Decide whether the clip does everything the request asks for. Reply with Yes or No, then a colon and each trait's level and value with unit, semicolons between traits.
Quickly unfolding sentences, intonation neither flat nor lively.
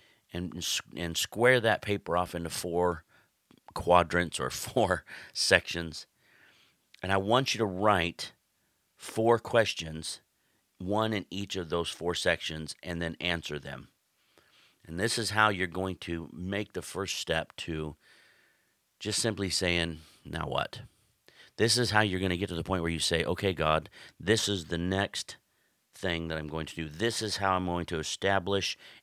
No: average, 165 wpm; average, 3.4 semitones